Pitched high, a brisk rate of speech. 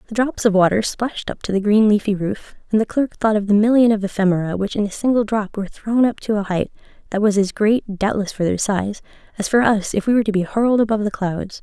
Yes: high, 210 Hz; fast, 265 wpm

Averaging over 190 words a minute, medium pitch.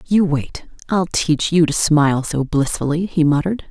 No: average, 180 wpm; medium, 160 Hz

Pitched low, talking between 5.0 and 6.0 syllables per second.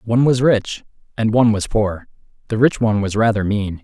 Yes: low, 110 Hz; 5.7 syllables/s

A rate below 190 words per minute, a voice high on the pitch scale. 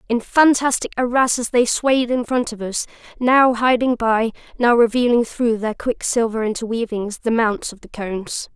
Yes: average, 155 wpm; high, 235 Hz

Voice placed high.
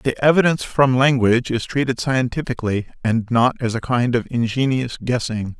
No: low, 125 Hz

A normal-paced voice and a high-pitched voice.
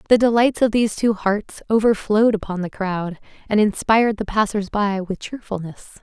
Yes: average, 170 wpm; high, 210 Hz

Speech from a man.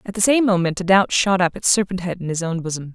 No: female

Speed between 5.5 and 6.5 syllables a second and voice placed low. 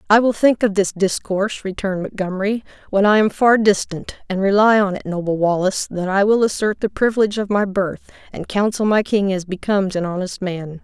No: 5.6 syllables/s; high, 200 Hz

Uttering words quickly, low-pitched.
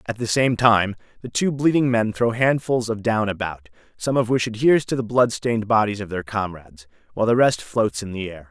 Yes: fast, 225 wpm; low, 110 Hz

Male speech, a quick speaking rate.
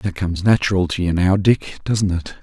Yes: male; fast, 225 wpm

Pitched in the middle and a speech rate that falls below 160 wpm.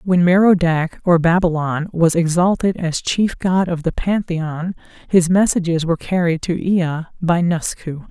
Yes: medium, 170 Hz; average, 150 wpm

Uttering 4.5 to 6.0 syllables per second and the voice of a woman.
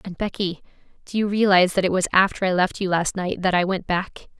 No: 6.3 syllables/s; female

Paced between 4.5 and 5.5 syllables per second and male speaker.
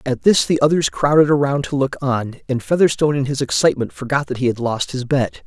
No: 5.9 syllables/s; male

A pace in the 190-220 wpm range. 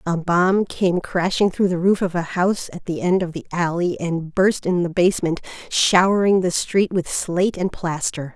Yes: average, 200 wpm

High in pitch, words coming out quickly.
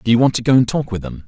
No: low, 115 Hz; fast, 425 wpm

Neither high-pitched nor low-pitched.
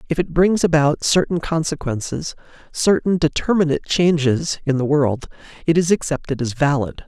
Yes: medium, 155 Hz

